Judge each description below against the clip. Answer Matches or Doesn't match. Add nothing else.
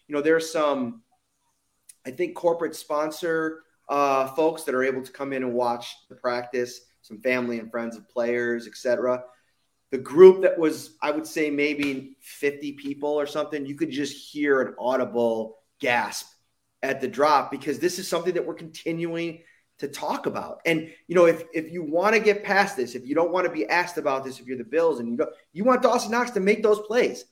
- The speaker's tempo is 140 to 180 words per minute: Doesn't match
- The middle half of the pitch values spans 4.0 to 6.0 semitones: Matches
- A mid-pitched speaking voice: Matches